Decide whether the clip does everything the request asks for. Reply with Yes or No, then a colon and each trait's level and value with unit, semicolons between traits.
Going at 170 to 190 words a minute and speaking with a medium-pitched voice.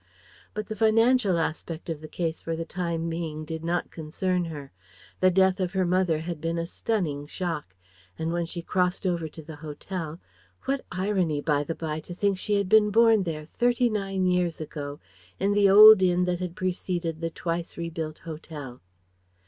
Yes: average, 185 wpm; medium, 175 Hz